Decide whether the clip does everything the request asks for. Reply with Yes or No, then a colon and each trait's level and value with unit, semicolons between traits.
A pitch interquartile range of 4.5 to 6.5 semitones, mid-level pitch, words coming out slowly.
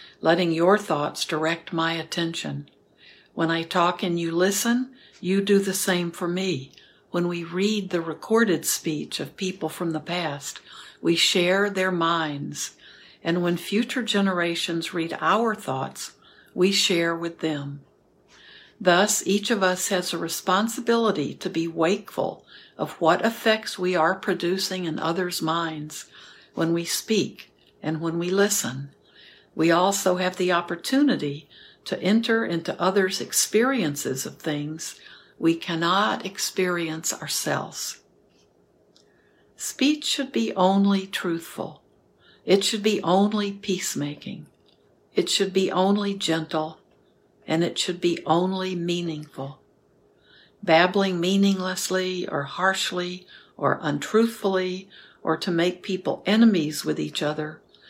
No: average, 3.1 semitones; medium, 180 Hz; slow, 125 wpm